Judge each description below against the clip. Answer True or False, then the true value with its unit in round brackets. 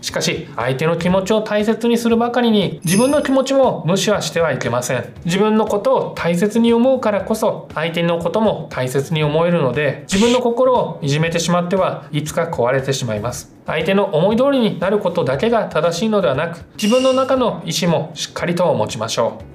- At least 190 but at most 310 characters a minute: False (410 characters per minute)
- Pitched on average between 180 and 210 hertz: True (185 Hz)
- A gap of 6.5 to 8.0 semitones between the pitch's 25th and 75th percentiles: False (6.0 semitones)